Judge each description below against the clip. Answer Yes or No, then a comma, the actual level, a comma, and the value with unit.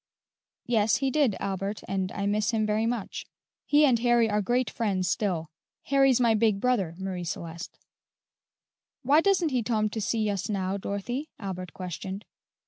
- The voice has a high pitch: Yes, high, 215 Hz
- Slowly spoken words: No, average, 160 wpm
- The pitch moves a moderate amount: Yes, average, 4.1 semitones